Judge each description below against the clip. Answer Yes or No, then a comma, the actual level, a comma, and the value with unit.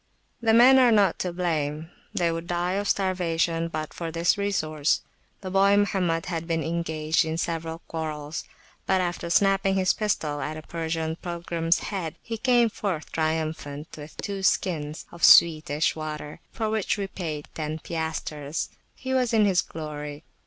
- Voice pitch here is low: No, medium, 165 Hz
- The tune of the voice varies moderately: Yes, average, 3.6 semitones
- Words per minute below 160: No, average, 165 wpm